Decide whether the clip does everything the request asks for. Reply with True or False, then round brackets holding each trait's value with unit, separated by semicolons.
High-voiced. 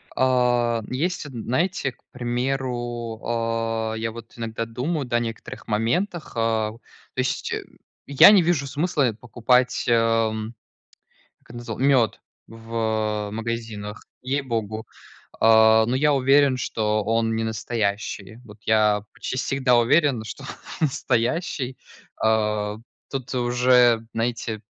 False (115 Hz)